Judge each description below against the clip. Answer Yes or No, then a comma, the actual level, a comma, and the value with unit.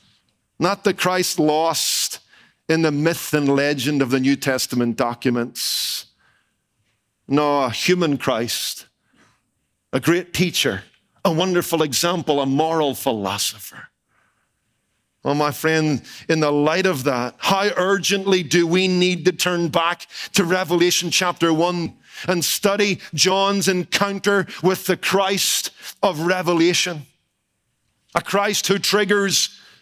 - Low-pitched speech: No, medium, 170 Hz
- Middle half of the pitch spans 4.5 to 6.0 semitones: Yes, average, 4.8 semitones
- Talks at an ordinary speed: No, slow, 120 wpm